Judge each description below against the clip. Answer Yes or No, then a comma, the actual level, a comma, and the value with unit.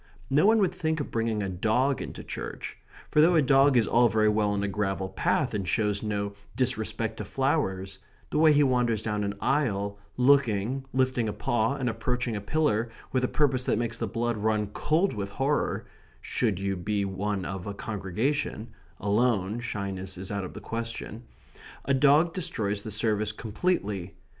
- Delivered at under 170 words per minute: No, average, 180 wpm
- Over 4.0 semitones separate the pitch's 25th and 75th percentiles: Yes, average, 4.6 semitones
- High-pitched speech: No, low, 110 Hz